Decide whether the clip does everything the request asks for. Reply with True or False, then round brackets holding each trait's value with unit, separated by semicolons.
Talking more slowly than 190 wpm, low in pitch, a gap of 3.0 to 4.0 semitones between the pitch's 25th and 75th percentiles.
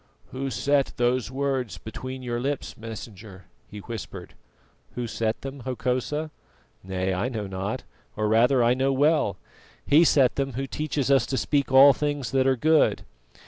True (160 wpm; 130 Hz; 3.5 semitones)